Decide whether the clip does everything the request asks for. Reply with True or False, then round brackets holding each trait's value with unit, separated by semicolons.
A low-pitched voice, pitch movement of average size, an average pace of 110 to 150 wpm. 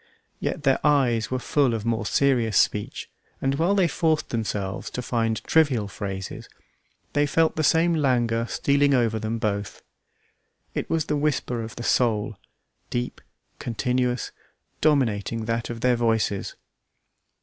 True (120 Hz; 4.3 semitones; 140 wpm)